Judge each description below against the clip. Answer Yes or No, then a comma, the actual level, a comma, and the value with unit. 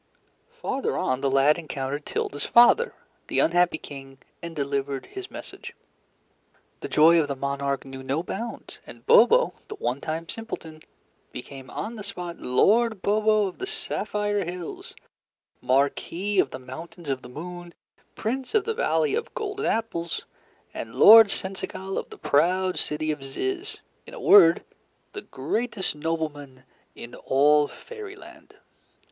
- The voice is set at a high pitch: No, medium, 170 Hz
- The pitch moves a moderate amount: No, wide, 8.0 semitones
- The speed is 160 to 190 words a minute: No, average, 145 wpm